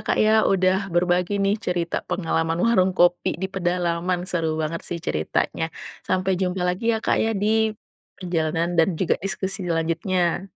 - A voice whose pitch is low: No, medium, 180 Hz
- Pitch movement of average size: No, narrow, 1.9 semitones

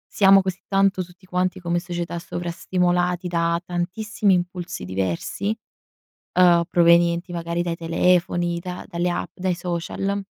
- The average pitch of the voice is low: No, medium, 175 Hz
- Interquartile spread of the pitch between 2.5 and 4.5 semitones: No, narrow, 1.2 semitones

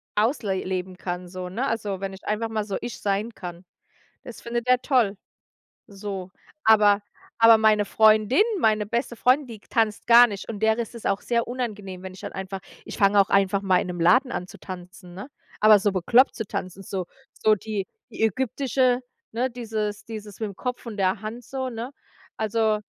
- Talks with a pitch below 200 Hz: No, high, 215 Hz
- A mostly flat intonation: No, average, 3.2 semitones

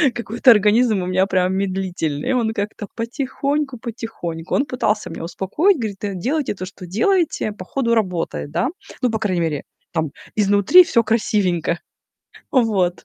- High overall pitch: Yes, high, 210 Hz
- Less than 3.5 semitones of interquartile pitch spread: No, average, 4.6 semitones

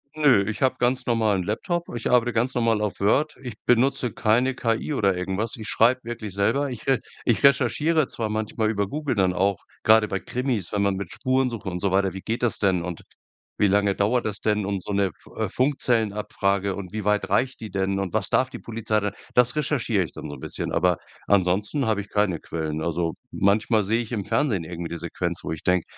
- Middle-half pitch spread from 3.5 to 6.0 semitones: Yes, average, 3.8 semitones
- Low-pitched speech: Yes, low, 105 Hz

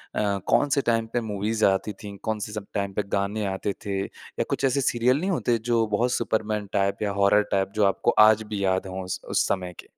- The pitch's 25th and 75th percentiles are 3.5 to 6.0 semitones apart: No, narrow, 2.4 semitones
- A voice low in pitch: Yes, low, 105 Hz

